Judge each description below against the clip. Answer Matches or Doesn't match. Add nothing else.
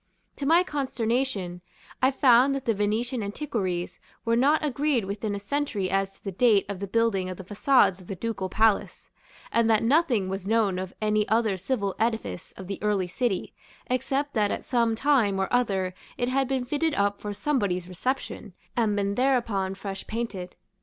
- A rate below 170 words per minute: Doesn't match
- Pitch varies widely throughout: Doesn't match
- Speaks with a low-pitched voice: Doesn't match